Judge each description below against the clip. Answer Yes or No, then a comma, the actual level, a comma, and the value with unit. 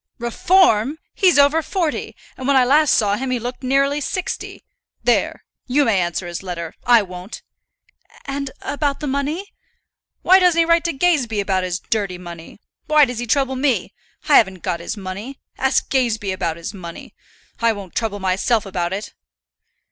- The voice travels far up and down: Yes, wide, 6.8 semitones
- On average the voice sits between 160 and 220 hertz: No, high, 240 Hz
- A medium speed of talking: Yes, average, 170 wpm